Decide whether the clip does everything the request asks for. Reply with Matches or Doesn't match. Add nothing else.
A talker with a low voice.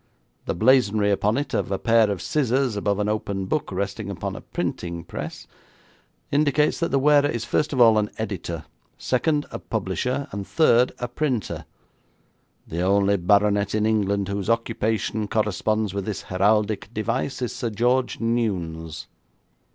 Matches